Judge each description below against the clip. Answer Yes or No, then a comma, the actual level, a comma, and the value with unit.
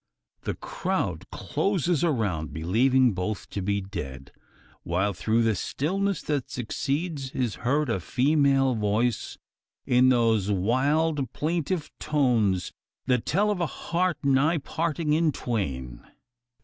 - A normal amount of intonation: No, wide, 6.9 semitones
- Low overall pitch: Yes, low, 130 Hz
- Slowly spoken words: Yes, slow, 125 wpm